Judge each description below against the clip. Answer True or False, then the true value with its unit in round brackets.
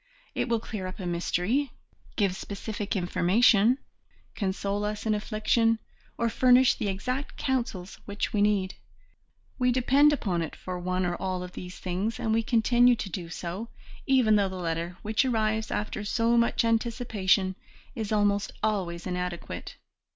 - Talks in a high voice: True (210 Hz)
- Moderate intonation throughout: True (3.9 semitones)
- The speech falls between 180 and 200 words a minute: False (155 wpm)